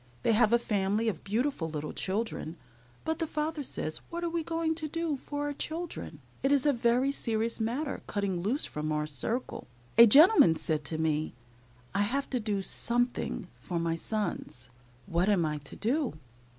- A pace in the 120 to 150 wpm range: No, average, 180 wpm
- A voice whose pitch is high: Yes, high, 230 Hz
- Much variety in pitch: Yes, wide, 8.8 semitones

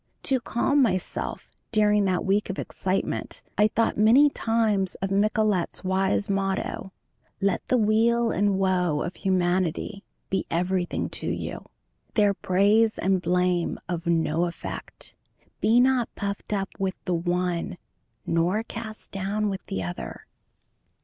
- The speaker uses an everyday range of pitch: Yes, average, 3.0 semitones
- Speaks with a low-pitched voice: No, high, 195 Hz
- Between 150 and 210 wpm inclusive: No, slow, 135 wpm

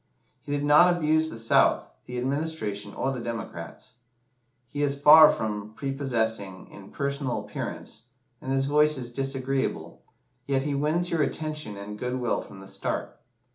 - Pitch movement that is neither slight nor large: Yes, average, 4.6 semitones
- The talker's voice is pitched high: No, low, 135 Hz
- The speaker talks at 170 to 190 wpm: No, average, 155 wpm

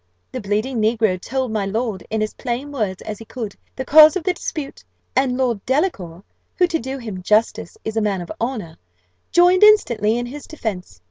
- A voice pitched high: Yes, high, 235 Hz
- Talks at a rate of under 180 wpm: No, average, 195 wpm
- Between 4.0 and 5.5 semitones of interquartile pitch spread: Yes, average, 4.7 semitones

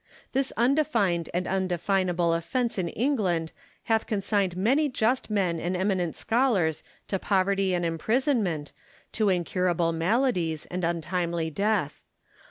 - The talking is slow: Yes, slow, 120 wpm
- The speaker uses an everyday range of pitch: Yes, average, 4.5 semitones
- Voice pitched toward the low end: No, medium, 185 Hz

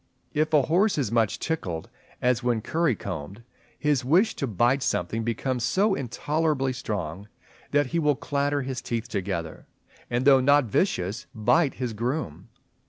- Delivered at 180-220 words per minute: No, average, 155 wpm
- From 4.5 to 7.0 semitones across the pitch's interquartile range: Yes, average, 5.1 semitones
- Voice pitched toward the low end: Yes, low, 125 Hz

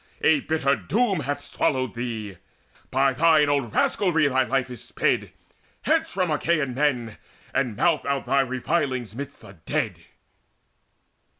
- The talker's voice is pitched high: No, medium, 140 Hz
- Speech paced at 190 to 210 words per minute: No, slow, 135 wpm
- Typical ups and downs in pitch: Yes, average, 3.5 semitones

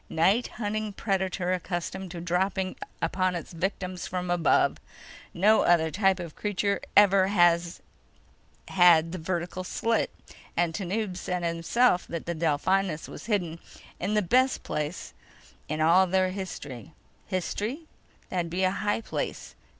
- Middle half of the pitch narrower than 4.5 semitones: Yes, narrow, 2.4 semitones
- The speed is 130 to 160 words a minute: Yes, average, 140 wpm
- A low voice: No, medium, 185 Hz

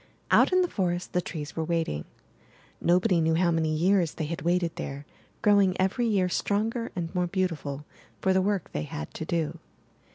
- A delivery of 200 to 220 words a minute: Yes, fast, 205 wpm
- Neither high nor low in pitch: Yes, medium, 175 Hz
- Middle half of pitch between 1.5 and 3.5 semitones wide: Yes, average, 2.9 semitones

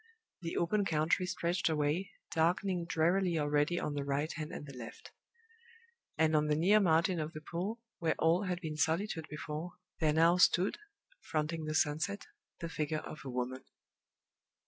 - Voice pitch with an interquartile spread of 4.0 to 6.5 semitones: No, average, 2.7 semitones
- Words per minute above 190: No, average, 165 wpm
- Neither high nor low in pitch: Yes, medium, 160 Hz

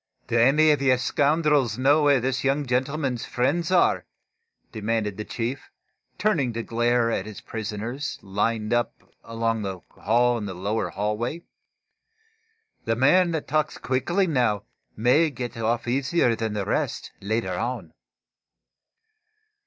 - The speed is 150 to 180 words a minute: No, slow, 135 wpm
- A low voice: Yes, low, 120 Hz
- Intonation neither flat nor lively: Yes, average, 4.1 semitones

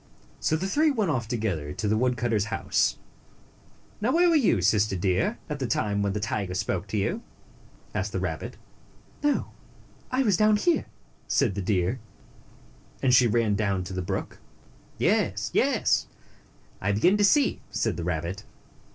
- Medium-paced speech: Yes, average, 170 wpm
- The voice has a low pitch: Yes, low, 110 Hz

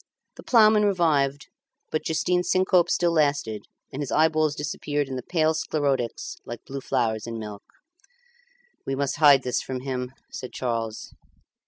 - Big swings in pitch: No, average, 4.0 semitones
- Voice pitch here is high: No, medium, 140 Hz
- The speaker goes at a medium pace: Yes, average, 150 wpm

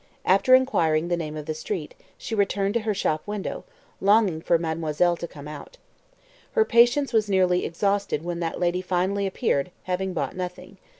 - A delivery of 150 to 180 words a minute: Yes, average, 175 wpm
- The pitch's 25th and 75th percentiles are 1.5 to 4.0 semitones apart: Yes, average, 3.6 semitones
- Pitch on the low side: No, medium, 185 Hz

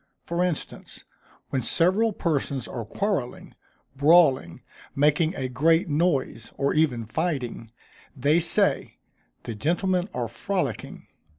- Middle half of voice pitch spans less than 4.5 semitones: No, wide, 5.6 semitones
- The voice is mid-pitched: Yes, medium, 150 Hz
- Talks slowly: Yes, slow, 110 wpm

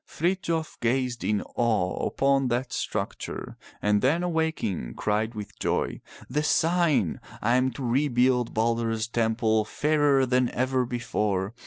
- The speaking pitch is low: Yes, low, 125 Hz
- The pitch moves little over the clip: No, average, 3.8 semitones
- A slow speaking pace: Yes, slow, 130 wpm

